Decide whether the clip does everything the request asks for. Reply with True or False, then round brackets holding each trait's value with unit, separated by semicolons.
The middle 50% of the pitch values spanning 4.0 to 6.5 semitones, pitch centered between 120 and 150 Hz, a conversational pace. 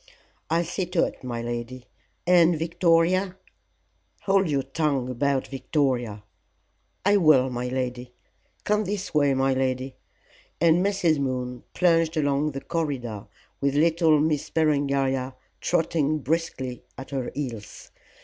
False (4.4 semitones; 140 Hz; 130 wpm)